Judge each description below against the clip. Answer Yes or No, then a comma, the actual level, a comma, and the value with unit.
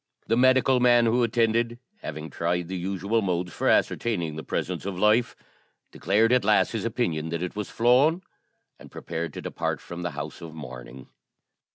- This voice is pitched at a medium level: No, low, 100 Hz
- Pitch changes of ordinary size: No, wide, 5.9 semitones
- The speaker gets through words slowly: No, average, 175 wpm